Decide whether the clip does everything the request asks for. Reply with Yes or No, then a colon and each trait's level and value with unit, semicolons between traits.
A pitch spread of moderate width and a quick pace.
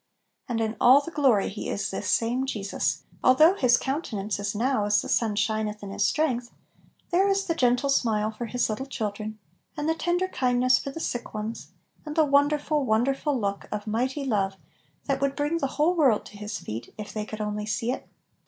Yes: average, 5.0 semitones; fast, 210 wpm